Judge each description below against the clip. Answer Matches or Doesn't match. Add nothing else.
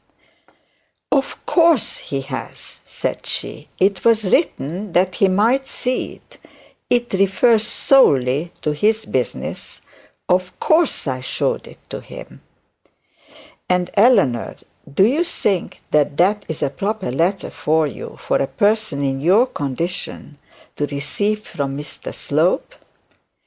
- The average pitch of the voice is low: Doesn't match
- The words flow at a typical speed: Doesn't match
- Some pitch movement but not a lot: Doesn't match